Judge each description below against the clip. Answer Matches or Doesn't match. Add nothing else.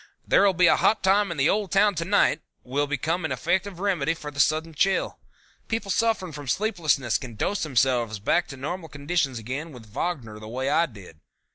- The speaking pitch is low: Doesn't match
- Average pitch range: Doesn't match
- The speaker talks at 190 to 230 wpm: Matches